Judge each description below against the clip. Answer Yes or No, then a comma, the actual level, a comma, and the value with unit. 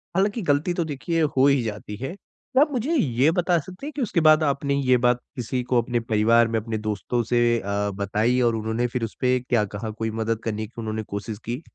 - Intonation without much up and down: No, average, 4.6 semitones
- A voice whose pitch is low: Yes, low, 120 Hz